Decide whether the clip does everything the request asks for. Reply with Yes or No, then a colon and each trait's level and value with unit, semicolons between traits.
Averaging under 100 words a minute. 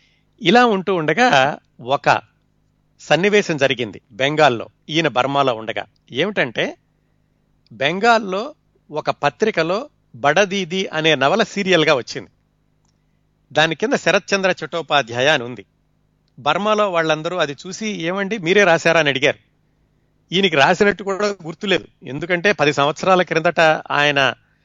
No: average, 105 wpm